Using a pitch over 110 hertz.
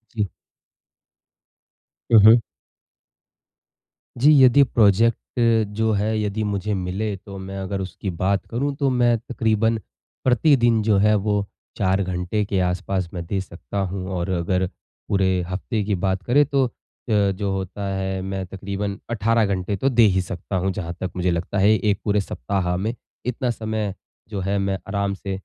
No: low, 100 Hz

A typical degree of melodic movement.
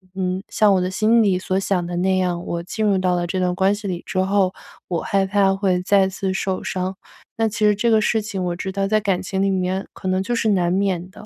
No: narrow, 1.6 semitones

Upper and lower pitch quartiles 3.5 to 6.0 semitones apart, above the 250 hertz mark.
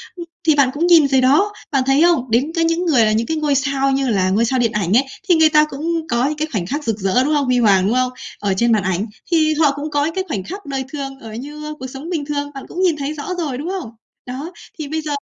Yes: average, 4.0 semitones; very high, 280 Hz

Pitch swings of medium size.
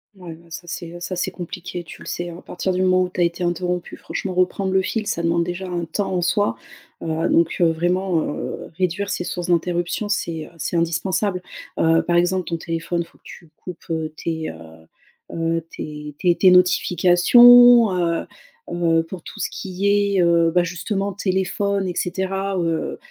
No: narrow, 2.0 semitones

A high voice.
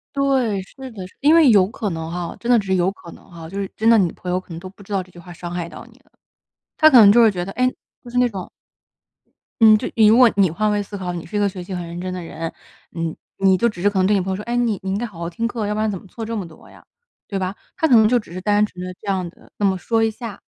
Yes: high, 200 Hz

